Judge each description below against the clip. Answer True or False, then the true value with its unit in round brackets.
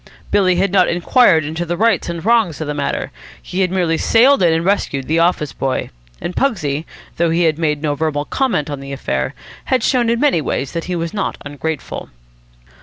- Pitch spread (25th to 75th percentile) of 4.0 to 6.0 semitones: True (4.6 semitones)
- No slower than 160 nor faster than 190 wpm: False (205 wpm)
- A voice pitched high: False (170 Hz)